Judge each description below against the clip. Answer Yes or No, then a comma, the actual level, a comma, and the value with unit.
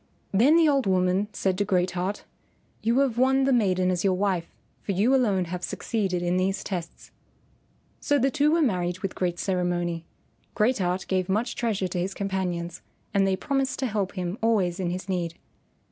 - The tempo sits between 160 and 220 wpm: Yes, average, 190 wpm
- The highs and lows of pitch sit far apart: No, average, 4.2 semitones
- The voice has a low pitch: No, high, 190 Hz